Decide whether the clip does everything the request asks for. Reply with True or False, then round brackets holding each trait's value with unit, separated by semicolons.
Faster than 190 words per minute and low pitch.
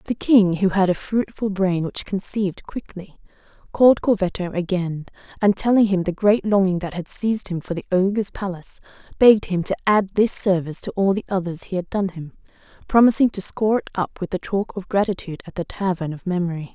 False (200 wpm; 190 Hz)